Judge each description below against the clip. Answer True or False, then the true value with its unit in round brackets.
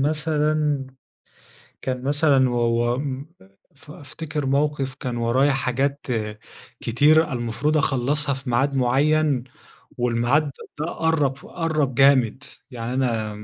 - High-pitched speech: False (135 Hz)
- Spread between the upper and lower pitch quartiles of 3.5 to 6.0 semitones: False (3.1 semitones)